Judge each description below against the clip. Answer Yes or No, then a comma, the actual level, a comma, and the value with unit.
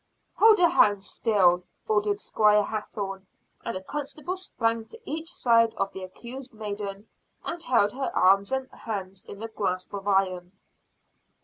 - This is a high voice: Yes, high, 210 Hz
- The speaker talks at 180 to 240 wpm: No, average, 150 wpm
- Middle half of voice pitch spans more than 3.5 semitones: Yes, average, 4.1 semitones